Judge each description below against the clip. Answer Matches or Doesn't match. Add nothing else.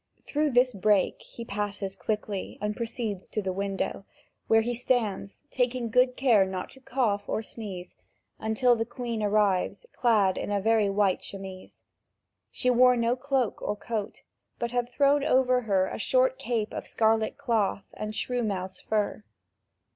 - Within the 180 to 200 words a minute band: Doesn't match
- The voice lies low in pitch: Doesn't match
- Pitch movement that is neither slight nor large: Matches